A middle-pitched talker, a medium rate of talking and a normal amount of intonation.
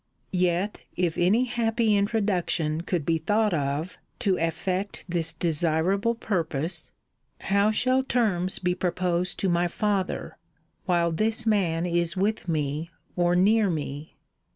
No: medium, 180 Hz; slow, 130 wpm; average, 3.8 semitones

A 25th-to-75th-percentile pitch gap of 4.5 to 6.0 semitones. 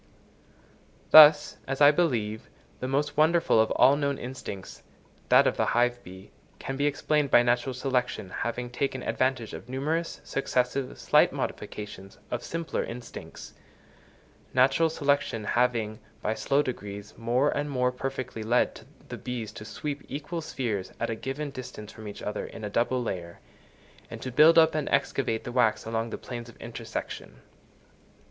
No: average, 3.9 semitones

